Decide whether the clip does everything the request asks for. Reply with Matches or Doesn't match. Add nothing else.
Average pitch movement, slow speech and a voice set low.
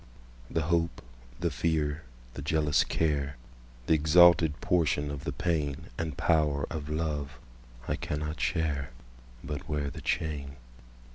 Doesn't match